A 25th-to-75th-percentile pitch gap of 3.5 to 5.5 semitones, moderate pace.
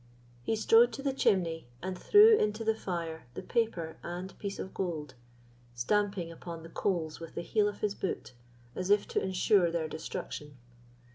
Yes: average, 4.1 semitones; average, 170 wpm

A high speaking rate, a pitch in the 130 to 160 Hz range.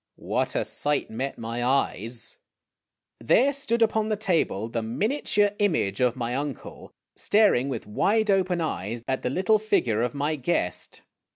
No: average, 155 wpm; medium, 140 Hz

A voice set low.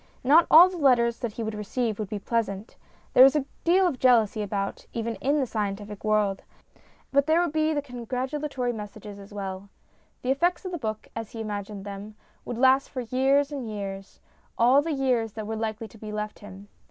No: high, 230 Hz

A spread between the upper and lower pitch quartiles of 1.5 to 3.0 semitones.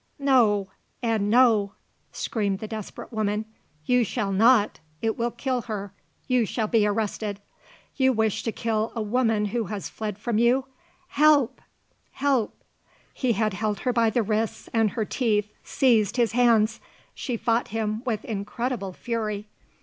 Yes: narrow, 2.4 semitones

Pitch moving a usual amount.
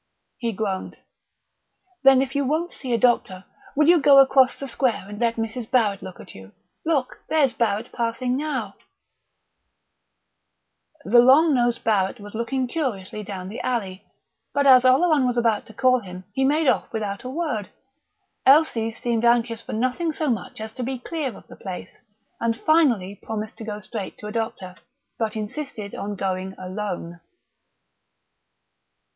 Yes: average, 4.4 semitones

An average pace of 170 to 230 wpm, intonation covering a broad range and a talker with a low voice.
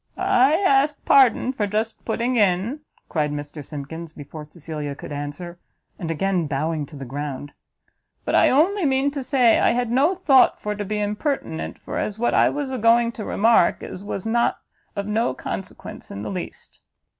No: average, 185 wpm; wide, 8.4 semitones; high, 210 Hz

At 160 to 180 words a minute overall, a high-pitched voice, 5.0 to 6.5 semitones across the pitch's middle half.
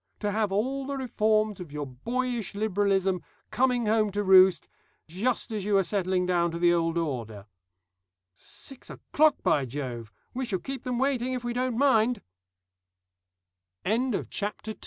Yes: average, 165 wpm; high, 210 Hz; wide, 5.5 semitones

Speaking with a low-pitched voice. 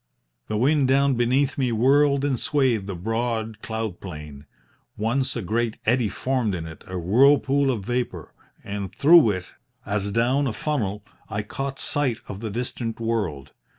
Yes: low, 115 Hz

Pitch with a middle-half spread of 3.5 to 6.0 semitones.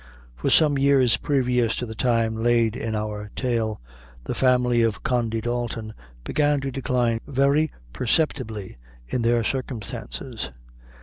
No: average, 2.9 semitones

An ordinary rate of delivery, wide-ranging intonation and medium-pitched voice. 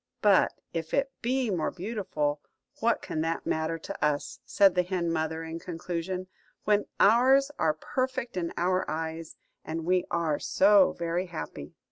No: average, 155 wpm; average, 4.0 semitones; medium, 175 Hz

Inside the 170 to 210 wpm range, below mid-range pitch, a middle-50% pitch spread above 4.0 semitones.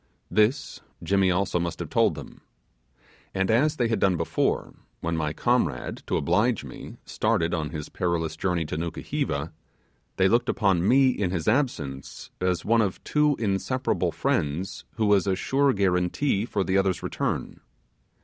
No: average, 160 wpm; very low, 95 Hz; average, 5.1 semitones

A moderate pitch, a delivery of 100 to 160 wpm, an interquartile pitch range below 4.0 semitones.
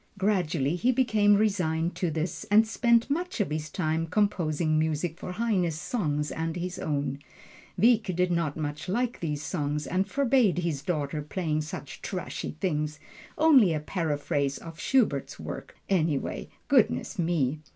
No: medium, 170 Hz; average, 145 wpm; average, 5.1 semitones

